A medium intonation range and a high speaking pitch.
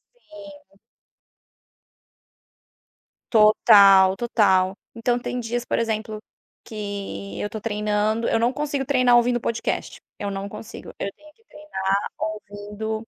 Yes: average, 3.0 semitones; high, 220 Hz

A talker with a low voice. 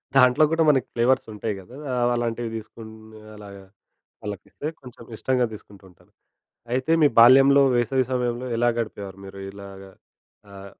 Yes: low, 115 Hz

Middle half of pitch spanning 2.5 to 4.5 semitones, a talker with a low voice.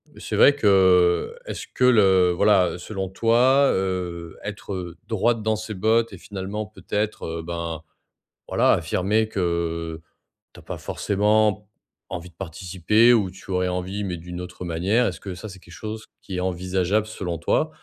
Yes: average, 3.4 semitones; very low, 95 Hz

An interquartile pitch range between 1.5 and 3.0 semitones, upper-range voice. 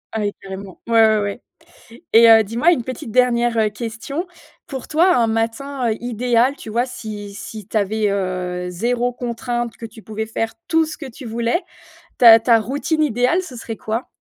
Yes: narrow, 2.4 semitones; high, 230 Hz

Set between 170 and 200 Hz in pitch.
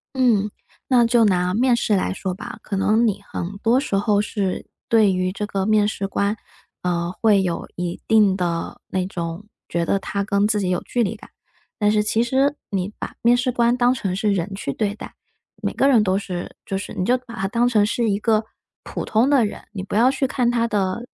No: high, 210 Hz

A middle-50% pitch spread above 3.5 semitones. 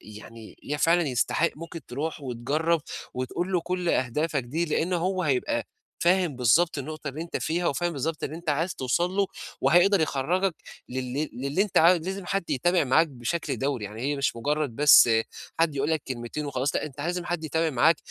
Yes: average, 4.4 semitones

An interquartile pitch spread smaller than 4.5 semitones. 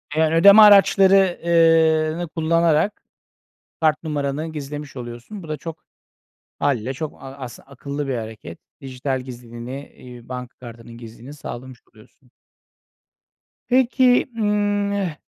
No: average, 5.1 semitones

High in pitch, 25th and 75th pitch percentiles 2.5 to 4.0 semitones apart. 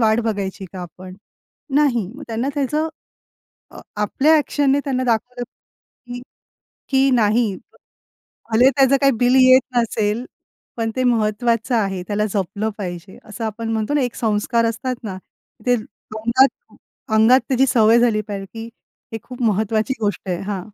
Yes: high, 225 Hz; average, 3.3 semitones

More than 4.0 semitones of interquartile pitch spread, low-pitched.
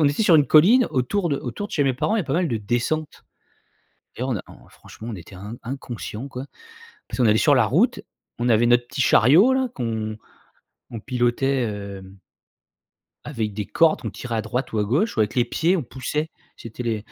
Yes: average, 5.1 semitones; low, 125 Hz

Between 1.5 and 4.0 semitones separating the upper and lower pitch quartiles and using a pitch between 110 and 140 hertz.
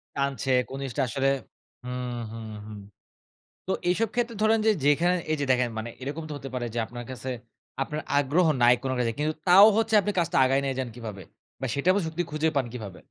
No: average, 5.3 semitones; low, 135 Hz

